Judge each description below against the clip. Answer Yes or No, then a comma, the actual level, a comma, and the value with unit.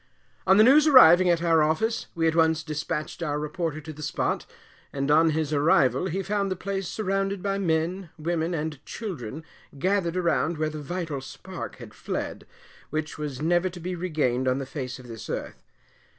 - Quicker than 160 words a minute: Yes, average, 185 wpm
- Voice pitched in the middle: Yes, medium, 160 Hz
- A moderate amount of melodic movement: Yes, average, 3.5 semitones